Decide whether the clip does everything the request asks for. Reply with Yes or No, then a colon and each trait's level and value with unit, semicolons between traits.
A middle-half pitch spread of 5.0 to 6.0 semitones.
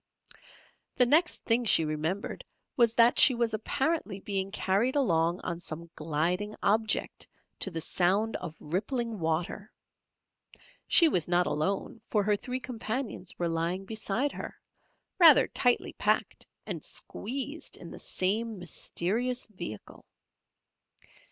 Yes: wide, 5.4 semitones